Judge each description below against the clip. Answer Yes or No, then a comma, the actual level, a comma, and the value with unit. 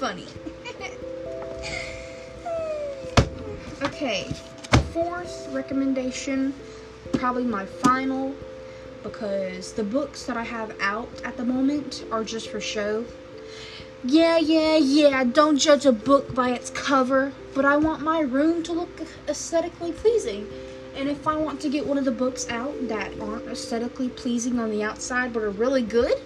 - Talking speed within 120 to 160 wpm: Yes, average, 140 wpm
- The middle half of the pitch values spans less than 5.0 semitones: Yes, average, 4.2 semitones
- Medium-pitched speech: No, very high, 265 Hz